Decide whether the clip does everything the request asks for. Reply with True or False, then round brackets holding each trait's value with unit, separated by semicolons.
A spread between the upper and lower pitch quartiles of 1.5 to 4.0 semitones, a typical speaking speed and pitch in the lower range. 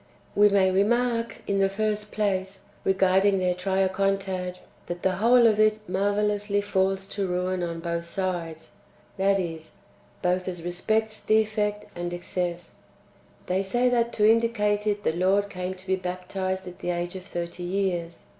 False (2.4 semitones; 160 wpm; 190 Hz)